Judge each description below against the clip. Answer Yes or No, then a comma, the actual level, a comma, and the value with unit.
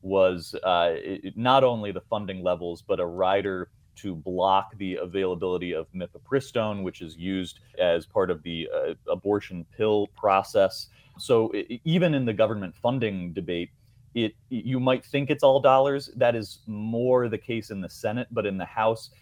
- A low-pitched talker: Yes, low, 110 Hz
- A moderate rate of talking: Yes, average, 170 wpm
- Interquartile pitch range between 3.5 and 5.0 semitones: Yes, average, 4.7 semitones